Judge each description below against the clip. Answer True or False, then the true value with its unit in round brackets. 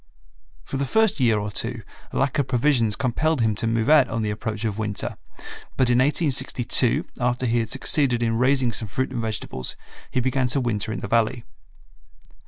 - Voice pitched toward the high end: False (120 Hz)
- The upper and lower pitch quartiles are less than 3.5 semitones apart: True (2.8 semitones)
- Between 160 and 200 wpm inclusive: True (190 wpm)